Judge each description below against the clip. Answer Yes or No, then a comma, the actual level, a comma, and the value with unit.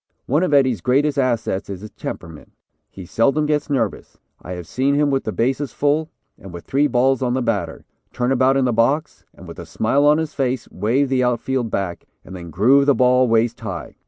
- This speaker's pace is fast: Yes, fast, 210 wpm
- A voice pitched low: Yes, low, 125 Hz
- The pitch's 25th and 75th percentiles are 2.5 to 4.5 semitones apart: Yes, average, 4.2 semitones